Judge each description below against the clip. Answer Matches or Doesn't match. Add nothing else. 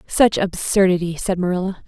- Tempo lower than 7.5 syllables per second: Matches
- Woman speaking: Matches